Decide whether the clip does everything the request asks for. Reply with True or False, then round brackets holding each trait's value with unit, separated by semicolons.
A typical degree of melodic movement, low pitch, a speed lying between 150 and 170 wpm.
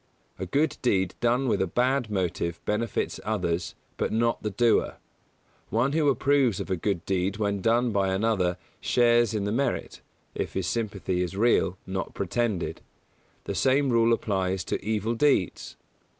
True (4.0 semitones; 105 Hz; 160 wpm)